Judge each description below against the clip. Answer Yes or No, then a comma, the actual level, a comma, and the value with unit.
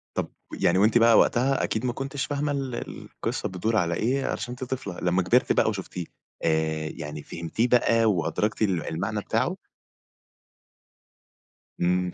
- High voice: No, low, 105 Hz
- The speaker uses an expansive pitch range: Yes, wide, 5.8 semitones